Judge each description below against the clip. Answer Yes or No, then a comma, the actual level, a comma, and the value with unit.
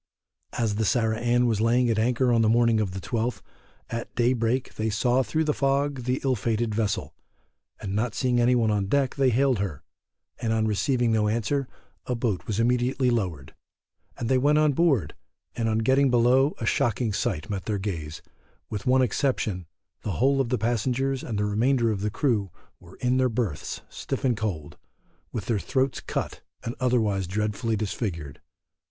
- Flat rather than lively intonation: No, average, 3.3 semitones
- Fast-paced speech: No, average, 185 wpm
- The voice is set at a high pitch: No, low, 115 Hz